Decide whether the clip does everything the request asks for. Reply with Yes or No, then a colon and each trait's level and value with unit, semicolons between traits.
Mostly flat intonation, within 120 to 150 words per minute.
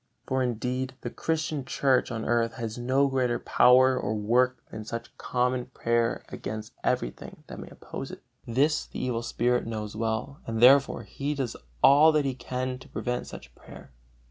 No: narrow, 2.3 semitones; average, 170 wpm